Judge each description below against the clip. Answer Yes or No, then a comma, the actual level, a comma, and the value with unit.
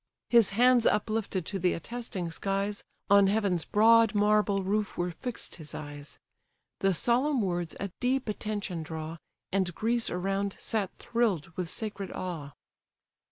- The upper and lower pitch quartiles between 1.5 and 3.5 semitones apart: No, average, 3.9 semitones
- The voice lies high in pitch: Yes, high, 200 Hz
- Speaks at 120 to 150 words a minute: Yes, average, 140 wpm